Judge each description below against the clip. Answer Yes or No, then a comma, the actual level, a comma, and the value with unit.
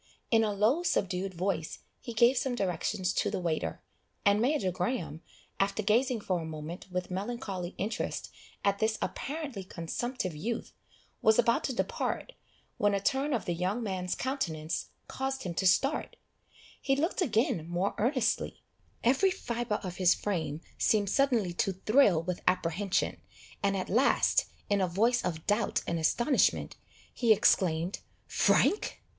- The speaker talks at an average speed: Yes, average, 150 wpm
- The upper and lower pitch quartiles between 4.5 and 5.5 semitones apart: Yes, average, 5.0 semitones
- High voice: Yes, high, 200 Hz